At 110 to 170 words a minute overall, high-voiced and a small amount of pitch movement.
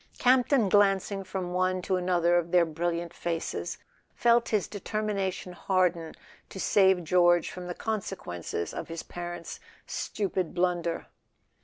No: slow, 135 wpm; medium, 180 Hz; narrow, 2.2 semitones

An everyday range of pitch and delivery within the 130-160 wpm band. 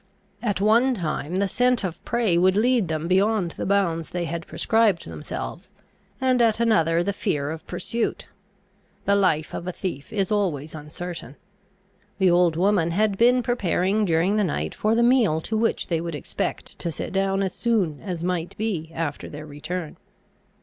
No: average, 4.7 semitones; average, 175 wpm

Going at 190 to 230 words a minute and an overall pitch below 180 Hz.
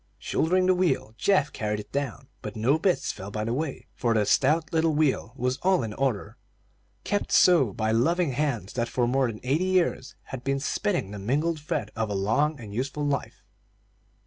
Yes: average, 195 wpm; low, 135 Hz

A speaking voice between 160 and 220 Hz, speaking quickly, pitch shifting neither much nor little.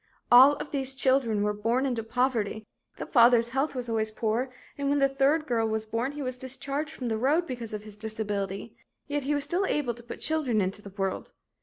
No: high, 245 Hz; fast, 215 wpm; average, 4.0 semitones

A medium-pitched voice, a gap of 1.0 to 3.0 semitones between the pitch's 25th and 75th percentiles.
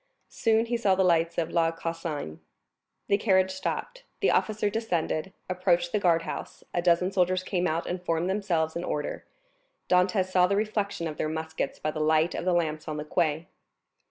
Yes: medium, 175 Hz; average, 2.7 semitones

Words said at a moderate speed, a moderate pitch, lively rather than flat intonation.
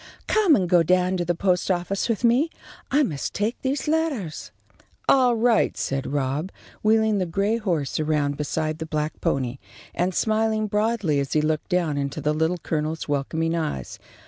Yes: average, 170 wpm; medium, 175 Hz; wide, 6.2 semitones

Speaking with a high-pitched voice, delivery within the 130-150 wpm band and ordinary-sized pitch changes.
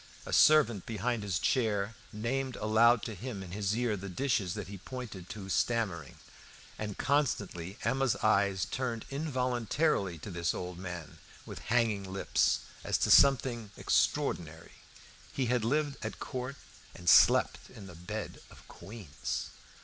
No: low, 110 Hz; average, 145 wpm; average, 4.6 semitones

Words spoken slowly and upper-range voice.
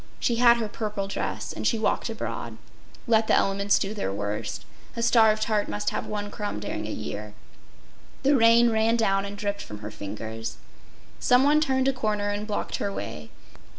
No: average, 185 wpm; high, 210 Hz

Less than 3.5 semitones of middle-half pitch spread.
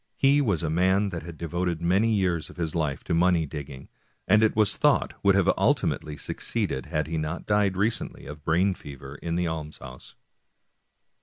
No: average, 3.8 semitones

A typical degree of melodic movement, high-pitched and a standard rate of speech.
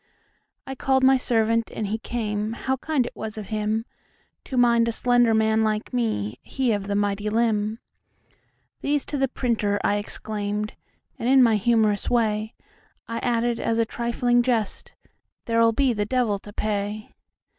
No: narrow, 2.3 semitones; high, 225 Hz; average, 145 wpm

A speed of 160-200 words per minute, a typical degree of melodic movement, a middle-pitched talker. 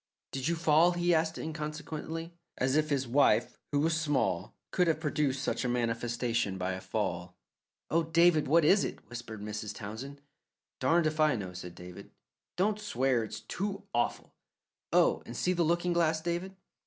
No: average, 165 wpm; wide, 5.7 semitones; medium, 150 Hz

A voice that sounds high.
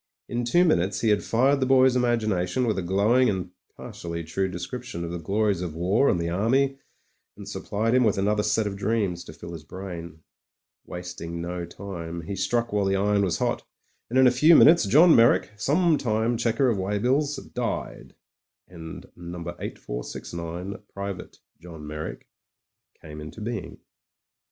No: low, 100 Hz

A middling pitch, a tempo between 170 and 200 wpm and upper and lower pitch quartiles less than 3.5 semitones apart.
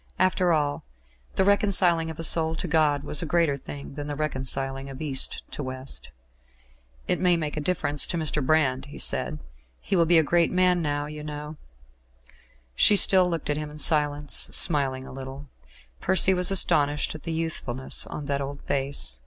Yes: medium, 150 Hz; average, 185 wpm; average, 2.9 semitones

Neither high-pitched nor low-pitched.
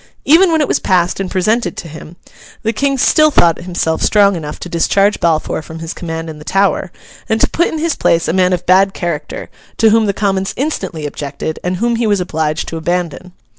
Yes: medium, 180 Hz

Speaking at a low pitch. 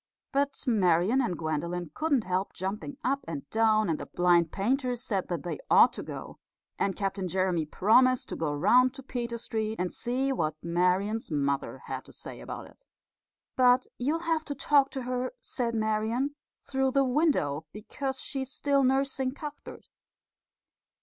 No: high, 230 Hz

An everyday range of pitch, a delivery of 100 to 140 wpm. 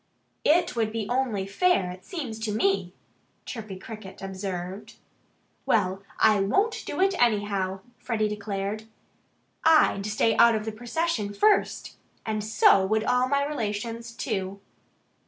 Yes: average, 3.5 semitones; slow, 135 wpm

